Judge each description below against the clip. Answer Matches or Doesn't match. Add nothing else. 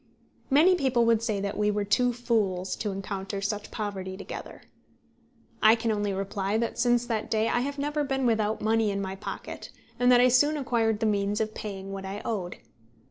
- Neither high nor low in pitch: Doesn't match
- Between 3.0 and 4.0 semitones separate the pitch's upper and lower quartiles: Matches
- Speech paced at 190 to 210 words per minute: Matches